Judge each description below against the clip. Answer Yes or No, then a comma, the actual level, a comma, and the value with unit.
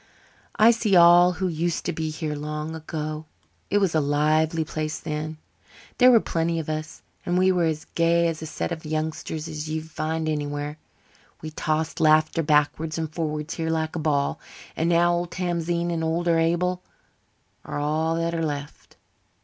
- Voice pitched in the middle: Yes, medium, 160 Hz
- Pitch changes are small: Yes, narrow, 1.6 semitones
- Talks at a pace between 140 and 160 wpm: No, average, 175 wpm